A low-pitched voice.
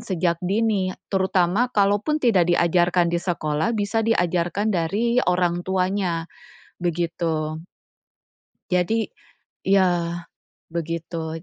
No: medium, 180 Hz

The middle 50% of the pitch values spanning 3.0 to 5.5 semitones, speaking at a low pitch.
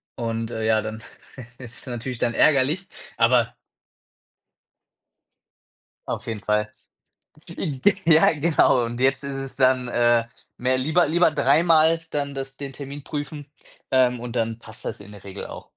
Yes: average, 3.9 semitones; low, 130 Hz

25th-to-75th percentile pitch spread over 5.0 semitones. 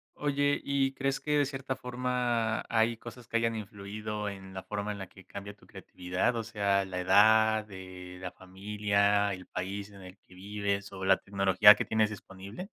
No: average, 3.1 semitones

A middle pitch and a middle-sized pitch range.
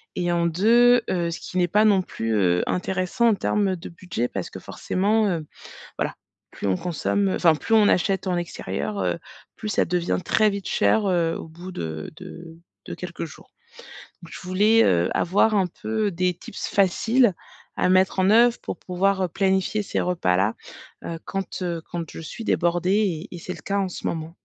Yes: medium, 180 Hz; average, 3.2 semitones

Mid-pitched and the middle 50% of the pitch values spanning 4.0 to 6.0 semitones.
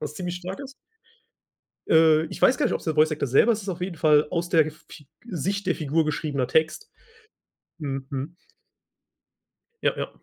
No: medium, 160 Hz; average, 3.3 semitones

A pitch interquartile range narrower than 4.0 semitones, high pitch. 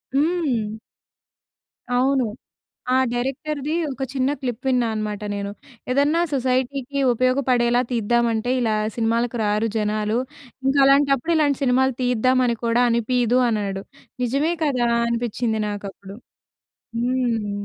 Yes: average, 3.1 semitones; high, 245 Hz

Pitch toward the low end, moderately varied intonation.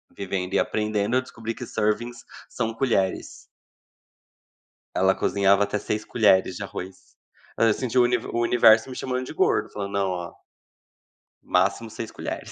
Yes: low, 110 Hz; average, 3.0 semitones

